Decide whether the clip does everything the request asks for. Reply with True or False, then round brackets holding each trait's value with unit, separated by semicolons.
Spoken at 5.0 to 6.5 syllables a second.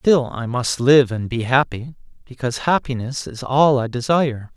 False (4.8 syllables/s)